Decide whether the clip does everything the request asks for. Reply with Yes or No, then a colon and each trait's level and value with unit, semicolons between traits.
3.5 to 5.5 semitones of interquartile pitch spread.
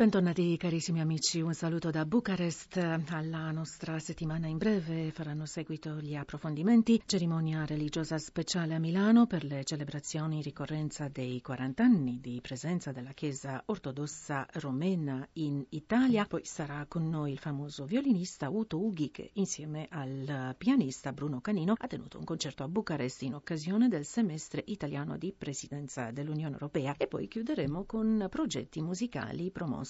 Yes: average, 3.9 semitones